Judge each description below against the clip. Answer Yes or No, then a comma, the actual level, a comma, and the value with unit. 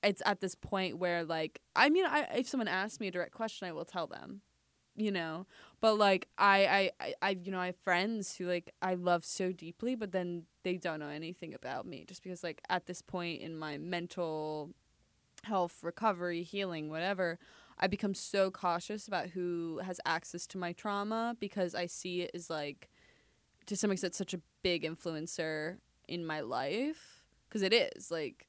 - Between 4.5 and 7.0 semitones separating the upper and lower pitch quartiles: No, average, 2.8 semitones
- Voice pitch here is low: No, medium, 180 Hz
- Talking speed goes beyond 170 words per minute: Yes, average, 190 wpm